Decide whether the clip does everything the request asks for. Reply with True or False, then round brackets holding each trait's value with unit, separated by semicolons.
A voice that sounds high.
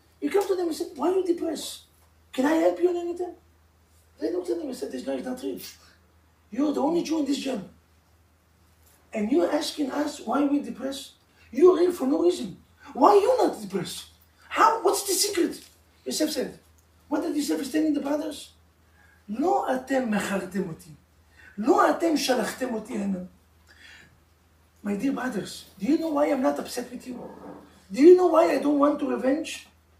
True (275 Hz)